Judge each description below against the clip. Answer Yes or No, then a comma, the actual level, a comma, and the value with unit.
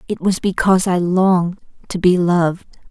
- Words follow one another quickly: No, average, 165 wpm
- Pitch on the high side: No, medium, 180 Hz